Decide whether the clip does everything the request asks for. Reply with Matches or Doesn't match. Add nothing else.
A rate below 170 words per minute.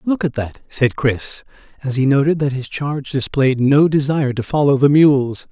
Doesn't match